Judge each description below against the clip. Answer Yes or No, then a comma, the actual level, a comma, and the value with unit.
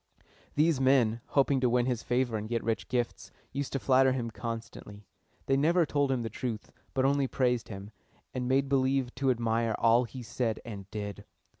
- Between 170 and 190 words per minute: Yes, average, 185 wpm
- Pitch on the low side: Yes, low, 125 Hz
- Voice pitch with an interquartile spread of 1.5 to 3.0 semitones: Yes, average, 2.7 semitones